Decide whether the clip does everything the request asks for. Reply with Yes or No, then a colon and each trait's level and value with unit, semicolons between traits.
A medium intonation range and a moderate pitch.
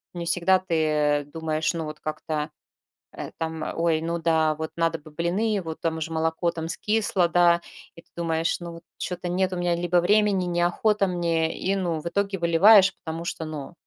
No: narrow, 1.8 semitones; medium, 170 Hz